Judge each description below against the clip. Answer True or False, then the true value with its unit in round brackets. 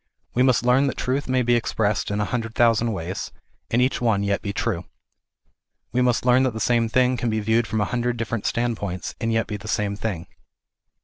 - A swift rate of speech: True (215 wpm)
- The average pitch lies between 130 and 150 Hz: False (115 Hz)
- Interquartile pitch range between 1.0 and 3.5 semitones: True (2.8 semitones)